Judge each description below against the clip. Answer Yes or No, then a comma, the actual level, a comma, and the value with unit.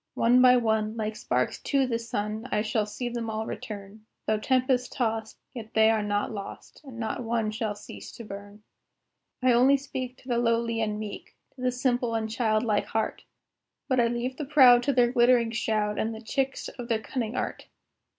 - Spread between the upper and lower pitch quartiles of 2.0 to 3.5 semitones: Yes, narrow, 2.5 semitones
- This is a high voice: Yes, high, 230 Hz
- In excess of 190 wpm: Yes, average, 200 wpm